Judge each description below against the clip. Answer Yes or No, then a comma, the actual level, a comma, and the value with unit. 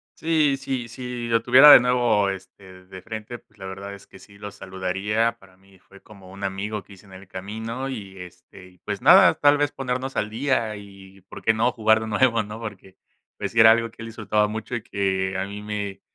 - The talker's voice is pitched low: Yes, low, 105 Hz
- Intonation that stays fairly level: No, average, 3.2 semitones